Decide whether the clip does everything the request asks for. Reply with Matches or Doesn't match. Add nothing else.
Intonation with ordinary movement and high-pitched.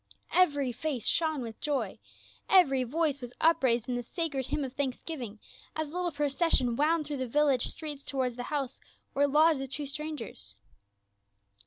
Matches